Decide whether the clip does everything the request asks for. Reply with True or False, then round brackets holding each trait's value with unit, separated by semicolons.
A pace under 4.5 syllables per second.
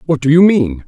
False (5.5 syllables/s)